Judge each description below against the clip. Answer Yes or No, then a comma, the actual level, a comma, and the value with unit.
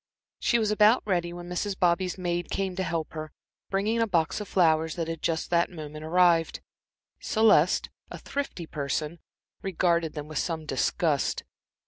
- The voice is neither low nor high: Yes, medium, 175 Hz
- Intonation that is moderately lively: Yes, average, 3.1 semitones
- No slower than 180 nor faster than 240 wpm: No, average, 160 wpm